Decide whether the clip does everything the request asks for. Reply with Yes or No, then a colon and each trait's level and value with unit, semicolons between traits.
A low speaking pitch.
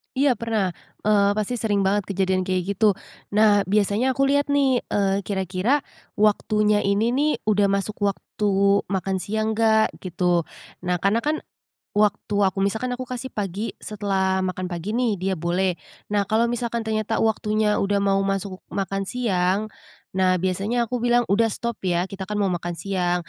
No: high, 205 Hz